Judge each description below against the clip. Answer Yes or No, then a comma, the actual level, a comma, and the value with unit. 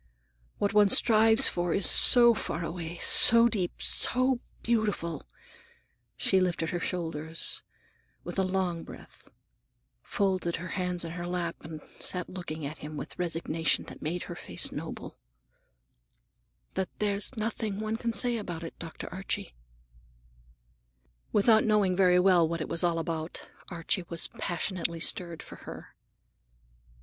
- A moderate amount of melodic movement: Yes, average, 3.6 semitones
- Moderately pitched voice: Yes, medium, 180 Hz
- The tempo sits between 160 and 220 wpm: No, average, 140 wpm